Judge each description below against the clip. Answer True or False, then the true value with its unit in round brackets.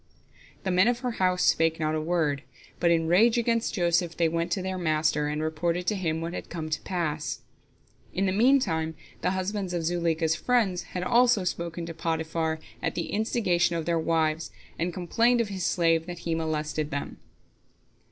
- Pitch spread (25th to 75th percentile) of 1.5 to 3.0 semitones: True (2.6 semitones)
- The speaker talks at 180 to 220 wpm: True (190 wpm)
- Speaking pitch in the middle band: True (170 Hz)